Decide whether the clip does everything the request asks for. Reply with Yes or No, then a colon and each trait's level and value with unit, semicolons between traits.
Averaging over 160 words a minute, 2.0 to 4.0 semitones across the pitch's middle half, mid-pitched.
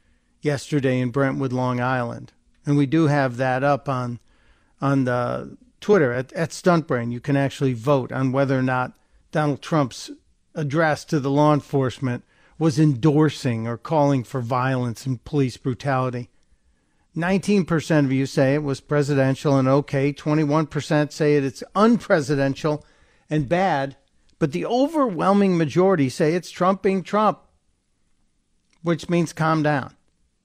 No: average, 145 wpm; average, 3.7 semitones; medium, 145 Hz